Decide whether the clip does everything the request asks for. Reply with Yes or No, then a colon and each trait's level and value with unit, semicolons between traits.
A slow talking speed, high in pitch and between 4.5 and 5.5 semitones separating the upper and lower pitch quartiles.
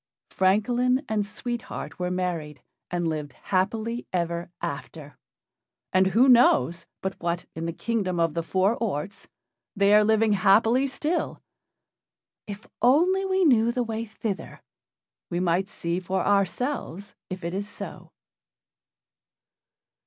Yes: slow, 130 wpm; high, 195 Hz; average, 5.0 semitones